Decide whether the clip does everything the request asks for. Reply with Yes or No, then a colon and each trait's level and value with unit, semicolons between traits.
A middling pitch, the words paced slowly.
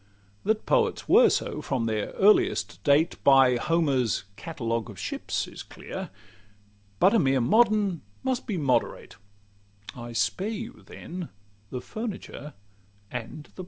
Yes: medium, 150 Hz; slow, 130 wpm